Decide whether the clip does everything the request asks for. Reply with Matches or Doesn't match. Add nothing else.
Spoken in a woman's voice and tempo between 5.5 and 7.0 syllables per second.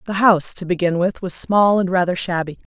Matches